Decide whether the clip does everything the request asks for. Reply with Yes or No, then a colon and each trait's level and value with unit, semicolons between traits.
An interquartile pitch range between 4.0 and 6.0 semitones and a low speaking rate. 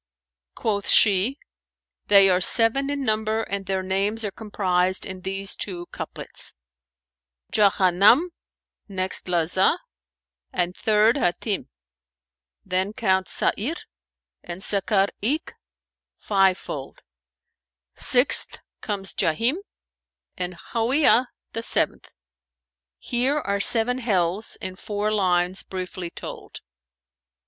No: average, 3.4 semitones; slow, 105 wpm